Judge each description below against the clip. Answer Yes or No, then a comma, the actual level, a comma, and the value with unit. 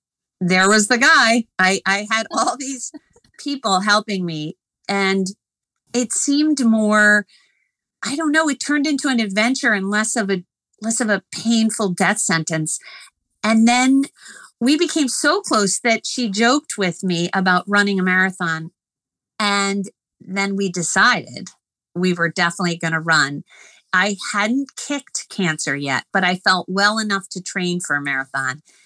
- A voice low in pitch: No, high, 205 Hz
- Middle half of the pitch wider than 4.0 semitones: Yes, average, 4.7 semitones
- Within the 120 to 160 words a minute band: Yes, average, 150 wpm